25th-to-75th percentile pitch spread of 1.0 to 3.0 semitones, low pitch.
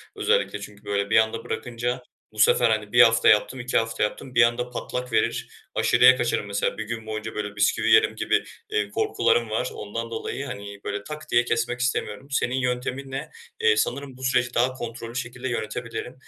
Yes: narrow, 2.5 semitones; low, 120 Hz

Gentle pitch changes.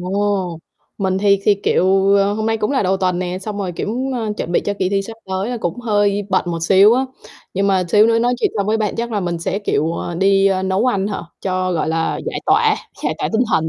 Yes: narrow, 2.3 semitones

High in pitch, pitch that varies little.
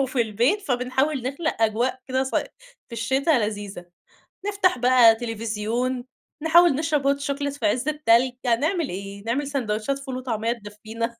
No: very high, 250 Hz; average, 3.8 semitones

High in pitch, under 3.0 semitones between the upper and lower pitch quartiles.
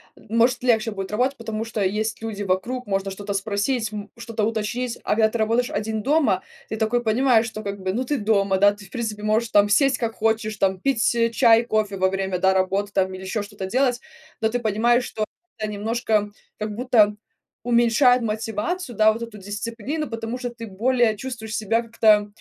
Yes: high, 220 Hz; narrow, 2.5 semitones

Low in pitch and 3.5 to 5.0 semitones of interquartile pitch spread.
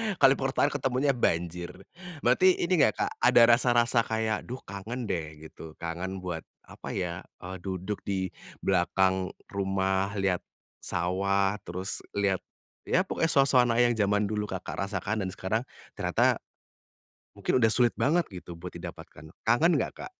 Yes: low, 100 Hz; average, 4.6 semitones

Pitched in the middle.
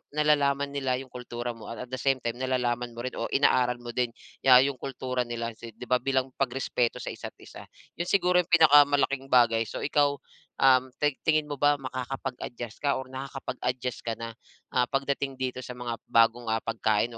No: low, 130 Hz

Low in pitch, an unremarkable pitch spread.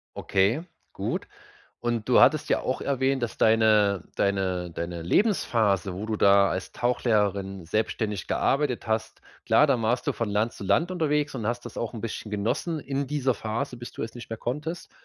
Yes: low, 115 Hz; average, 4.7 semitones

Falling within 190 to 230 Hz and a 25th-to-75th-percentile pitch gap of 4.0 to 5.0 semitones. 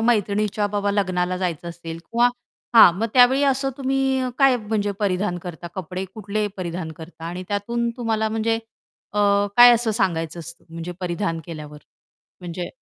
Yes: high, 200 Hz; average, 4.6 semitones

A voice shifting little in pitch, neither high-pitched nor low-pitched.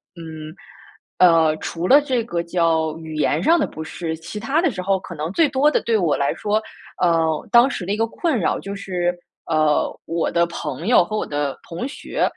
No: wide, 5.5 semitones; medium, 175 Hz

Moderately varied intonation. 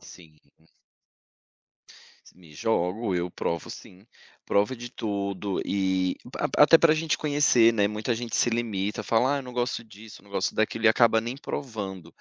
Yes: average, 3.9 semitones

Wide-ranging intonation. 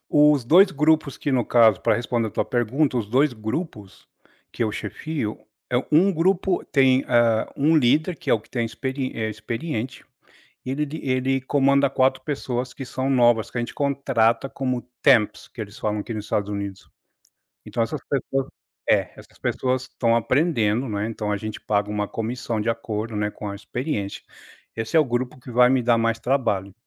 No: average, 3.8 semitones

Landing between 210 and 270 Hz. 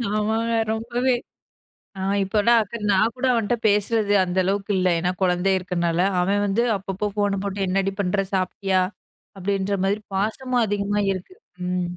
No: high, 200 Hz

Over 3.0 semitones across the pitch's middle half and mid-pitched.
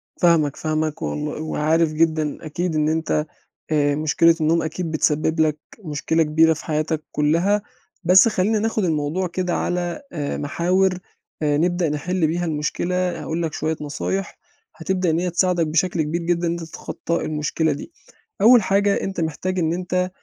No: average, 2.7 semitones; medium, 165 Hz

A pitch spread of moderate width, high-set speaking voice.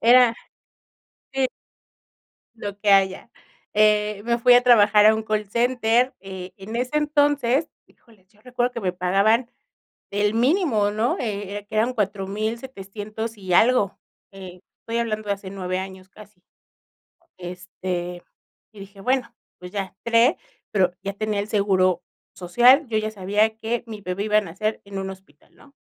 Yes: average, 3.3 semitones; high, 210 Hz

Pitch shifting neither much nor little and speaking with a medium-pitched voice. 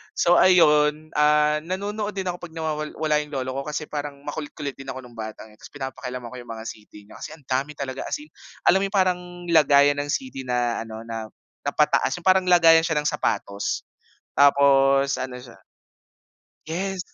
Yes: average, 3.8 semitones; medium, 145 Hz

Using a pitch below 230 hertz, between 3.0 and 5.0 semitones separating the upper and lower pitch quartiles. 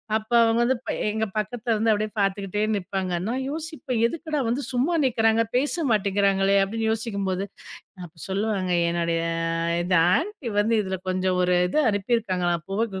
Yes: high, 215 Hz; average, 3.5 semitones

